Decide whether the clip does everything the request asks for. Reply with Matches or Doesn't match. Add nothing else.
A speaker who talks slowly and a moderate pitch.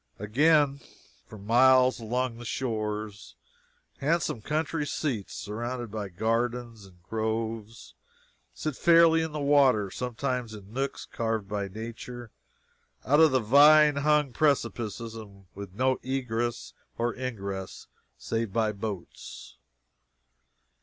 Doesn't match